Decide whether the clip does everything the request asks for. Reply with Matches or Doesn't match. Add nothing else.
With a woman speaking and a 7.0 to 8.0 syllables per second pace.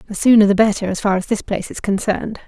Matches